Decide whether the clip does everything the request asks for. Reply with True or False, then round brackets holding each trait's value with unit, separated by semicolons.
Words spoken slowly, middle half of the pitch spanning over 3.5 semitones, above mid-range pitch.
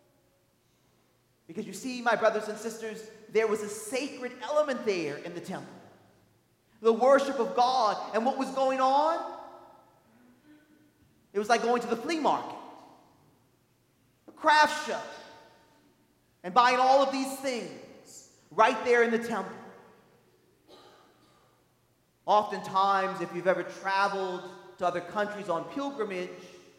True (130 wpm; 5.2 semitones; 225 Hz)